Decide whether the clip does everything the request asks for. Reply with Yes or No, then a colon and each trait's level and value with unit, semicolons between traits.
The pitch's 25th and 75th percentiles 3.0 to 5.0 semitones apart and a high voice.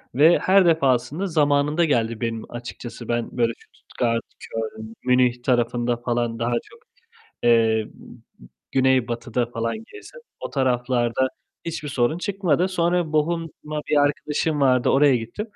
No: average, 4.6 semitones; low, 130 Hz